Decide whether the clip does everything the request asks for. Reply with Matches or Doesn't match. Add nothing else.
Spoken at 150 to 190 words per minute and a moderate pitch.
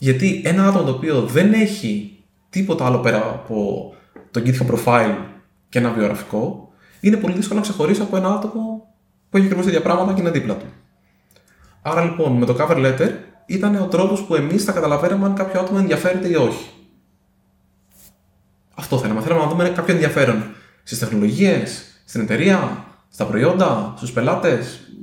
Matches